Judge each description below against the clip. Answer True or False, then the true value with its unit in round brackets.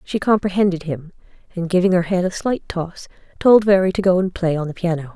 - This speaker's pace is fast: True (220 wpm)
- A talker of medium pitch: True (180 Hz)